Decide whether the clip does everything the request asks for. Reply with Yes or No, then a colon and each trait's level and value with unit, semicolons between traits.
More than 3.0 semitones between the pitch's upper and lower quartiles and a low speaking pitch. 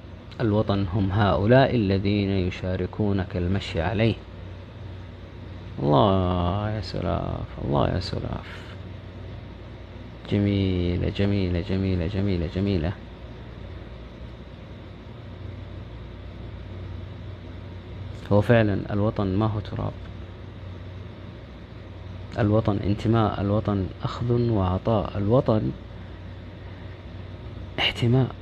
No: narrow, 2.5 semitones; low, 100 Hz